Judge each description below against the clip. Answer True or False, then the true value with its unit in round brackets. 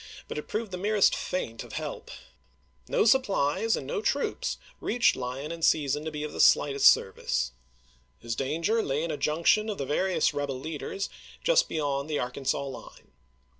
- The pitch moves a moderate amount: False (6.1 semitones)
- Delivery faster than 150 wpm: True (180 wpm)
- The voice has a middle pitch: True (150 Hz)